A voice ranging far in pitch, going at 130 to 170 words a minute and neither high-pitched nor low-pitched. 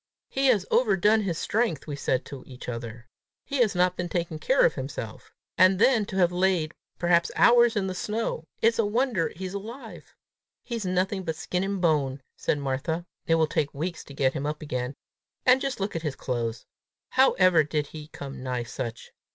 No: wide, 6.0 semitones; average, 195 wpm; medium, 175 Hz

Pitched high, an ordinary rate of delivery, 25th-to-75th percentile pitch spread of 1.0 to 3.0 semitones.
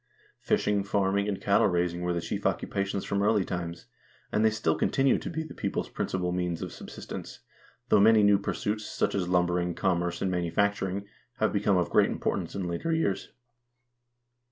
No: low, 100 Hz; average, 175 wpm; average, 2.7 semitones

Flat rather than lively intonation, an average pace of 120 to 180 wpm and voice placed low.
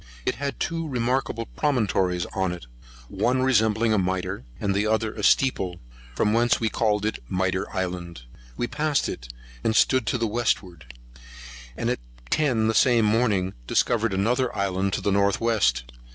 No: average, 4.2 semitones; average, 165 wpm; low, 110 Hz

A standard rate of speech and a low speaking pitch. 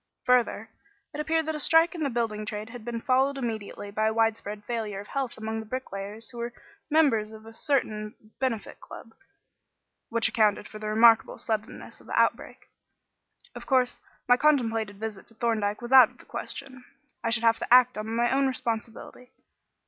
No: average, 185 wpm; high, 230 Hz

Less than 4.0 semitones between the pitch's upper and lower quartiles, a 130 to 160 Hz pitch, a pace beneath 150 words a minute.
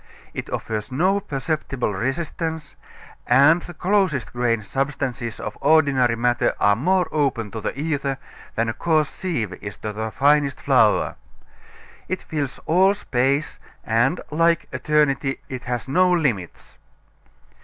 No: average, 4.9 semitones; medium, 140 Hz; slow, 135 wpm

